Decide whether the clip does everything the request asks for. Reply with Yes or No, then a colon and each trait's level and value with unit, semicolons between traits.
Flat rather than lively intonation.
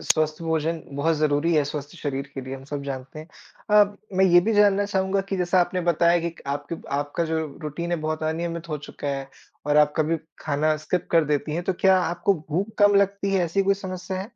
No: average, 4.1 semitones